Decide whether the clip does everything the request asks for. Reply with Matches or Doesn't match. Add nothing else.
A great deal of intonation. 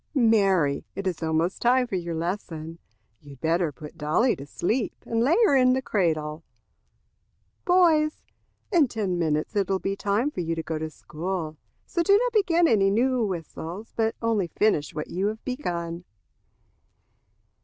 Matches